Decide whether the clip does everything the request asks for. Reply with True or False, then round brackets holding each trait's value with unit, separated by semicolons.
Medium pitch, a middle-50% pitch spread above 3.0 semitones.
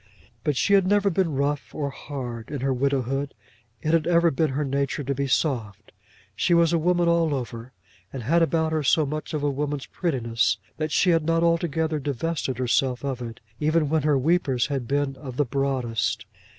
True (145 Hz; 3.7 semitones)